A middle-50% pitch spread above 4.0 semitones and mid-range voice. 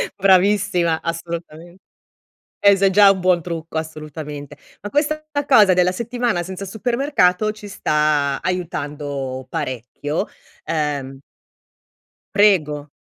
Yes: average, 4.9 semitones; medium, 175 Hz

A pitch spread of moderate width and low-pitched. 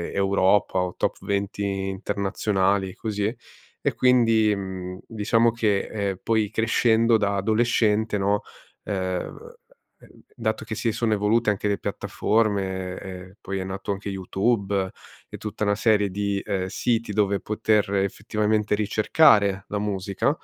No: narrow, 2.0 semitones; low, 100 Hz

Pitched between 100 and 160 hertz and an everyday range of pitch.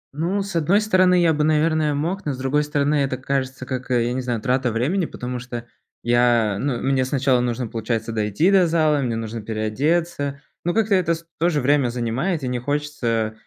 Yes: low, 135 Hz; average, 4.8 semitones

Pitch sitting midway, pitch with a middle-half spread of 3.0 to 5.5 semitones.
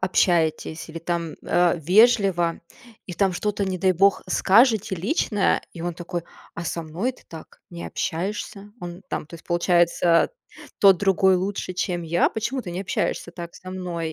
No: medium, 180 Hz; narrow, 2.5 semitones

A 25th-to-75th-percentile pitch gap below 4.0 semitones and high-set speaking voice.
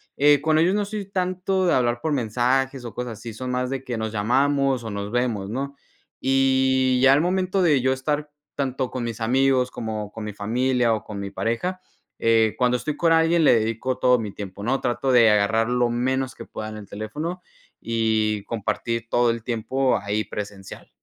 No: average, 3.5 semitones; low, 125 Hz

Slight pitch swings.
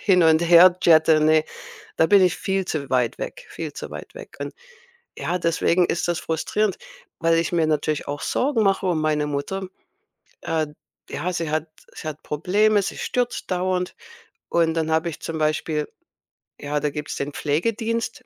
No: average, 3.2 semitones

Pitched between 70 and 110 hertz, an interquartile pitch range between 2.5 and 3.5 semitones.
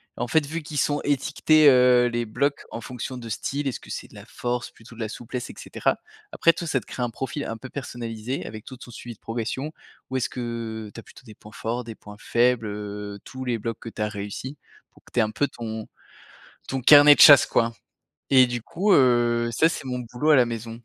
No: low, 120 Hz; average, 2.8 semitones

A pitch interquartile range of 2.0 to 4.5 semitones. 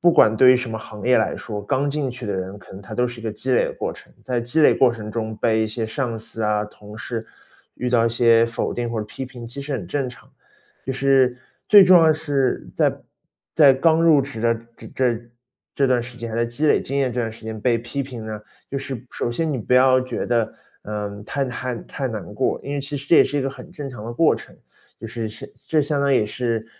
Yes: average, 3.5 semitones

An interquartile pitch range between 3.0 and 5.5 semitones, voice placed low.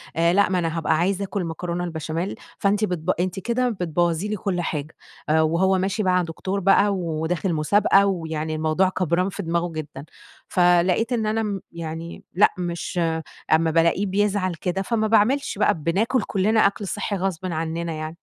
No: average, 3.3 semitones; medium, 180 Hz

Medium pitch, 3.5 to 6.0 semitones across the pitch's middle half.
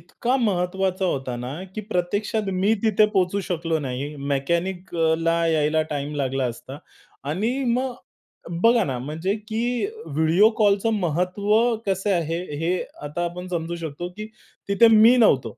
Yes: medium, 175 Hz; average, 4.6 semitones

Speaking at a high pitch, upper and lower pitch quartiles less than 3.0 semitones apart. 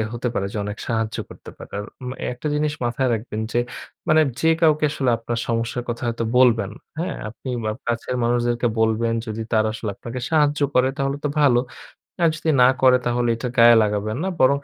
No: low, 120 Hz; narrow, 2.6 semitones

